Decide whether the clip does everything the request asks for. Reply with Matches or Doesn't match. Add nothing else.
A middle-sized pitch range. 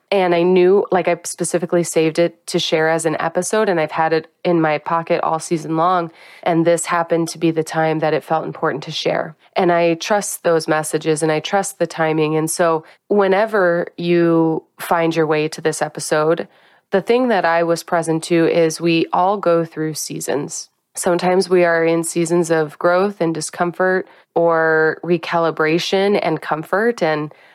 Doesn't match